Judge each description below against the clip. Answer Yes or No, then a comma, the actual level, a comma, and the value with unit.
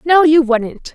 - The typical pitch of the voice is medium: No, very high, 290 Hz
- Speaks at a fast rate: No, average, 190 wpm